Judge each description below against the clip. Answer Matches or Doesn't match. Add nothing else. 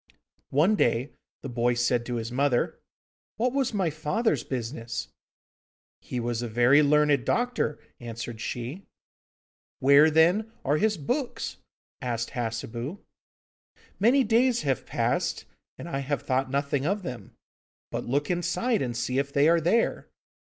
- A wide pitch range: Matches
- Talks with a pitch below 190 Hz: Matches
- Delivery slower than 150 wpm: Matches